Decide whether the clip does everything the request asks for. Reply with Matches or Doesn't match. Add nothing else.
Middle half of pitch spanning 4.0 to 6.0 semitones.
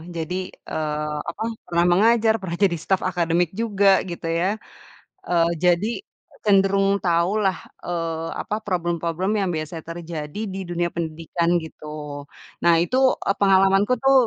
Doesn't match